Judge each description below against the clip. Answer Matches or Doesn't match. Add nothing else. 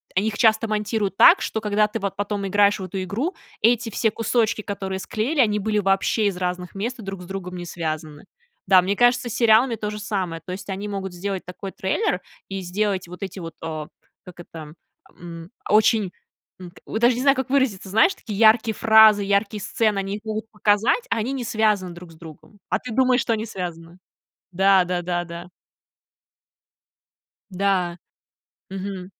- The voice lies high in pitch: Matches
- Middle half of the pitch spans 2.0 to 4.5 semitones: Matches